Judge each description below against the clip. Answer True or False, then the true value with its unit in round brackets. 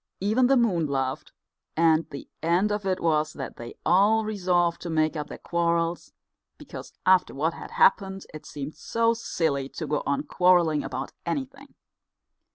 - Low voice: False (170 Hz)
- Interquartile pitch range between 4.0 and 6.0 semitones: True (4.4 semitones)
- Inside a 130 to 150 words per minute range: False (165 wpm)